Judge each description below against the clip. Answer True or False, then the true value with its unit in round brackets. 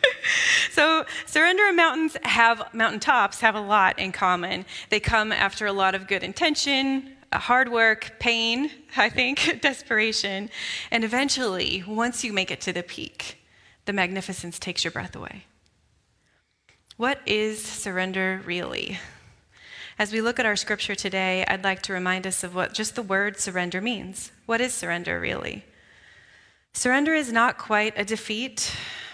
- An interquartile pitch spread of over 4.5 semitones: True (5.2 semitones)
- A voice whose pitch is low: False (220 Hz)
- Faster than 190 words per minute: False (150 wpm)